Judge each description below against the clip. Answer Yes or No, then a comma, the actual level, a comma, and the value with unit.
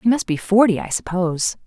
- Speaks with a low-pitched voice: No, high, 200 Hz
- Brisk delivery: Yes, fast, 215 wpm